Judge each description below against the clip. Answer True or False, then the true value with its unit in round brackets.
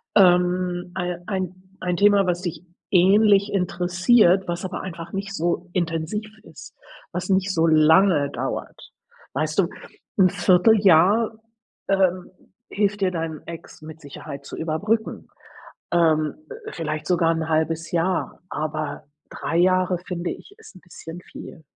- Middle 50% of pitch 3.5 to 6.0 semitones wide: False (2.7 semitones)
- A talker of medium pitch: True (180 Hz)